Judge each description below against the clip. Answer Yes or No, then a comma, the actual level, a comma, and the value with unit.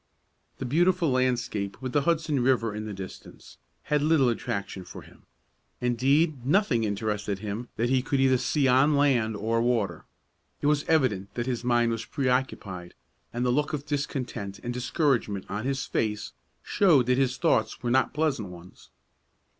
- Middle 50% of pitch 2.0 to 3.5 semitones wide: No, average, 4.4 semitones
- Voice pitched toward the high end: No, low, 125 Hz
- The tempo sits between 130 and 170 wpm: Yes, average, 165 wpm